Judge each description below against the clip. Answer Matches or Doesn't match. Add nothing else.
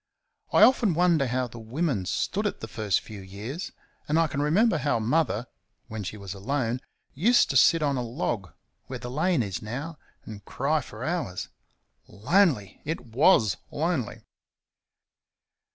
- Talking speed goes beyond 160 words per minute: Doesn't match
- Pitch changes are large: Matches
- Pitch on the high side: Doesn't match